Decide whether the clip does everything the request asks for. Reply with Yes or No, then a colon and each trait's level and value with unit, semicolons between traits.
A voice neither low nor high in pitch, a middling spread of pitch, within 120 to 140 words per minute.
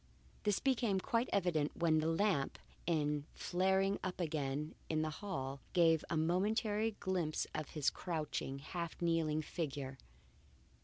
Yes: medium, 165 Hz; average, 3.9 semitones; slow, 135 wpm